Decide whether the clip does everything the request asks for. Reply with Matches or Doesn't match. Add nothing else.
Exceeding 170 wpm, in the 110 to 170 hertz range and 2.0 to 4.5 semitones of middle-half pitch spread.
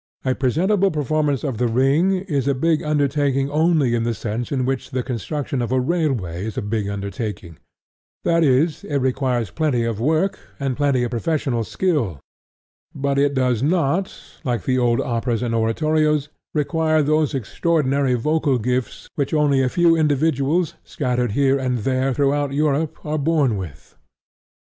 Doesn't match